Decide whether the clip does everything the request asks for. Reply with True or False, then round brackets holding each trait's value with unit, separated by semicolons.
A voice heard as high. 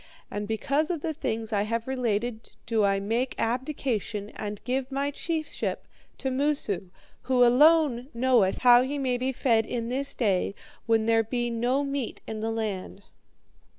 True (240 Hz)